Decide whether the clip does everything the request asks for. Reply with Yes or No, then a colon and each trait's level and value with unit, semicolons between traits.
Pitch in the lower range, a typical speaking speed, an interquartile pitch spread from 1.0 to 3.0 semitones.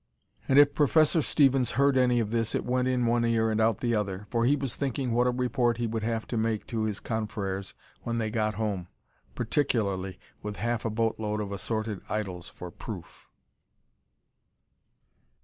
Yes: low, 115 Hz; average, 180 wpm; average, 2.7 semitones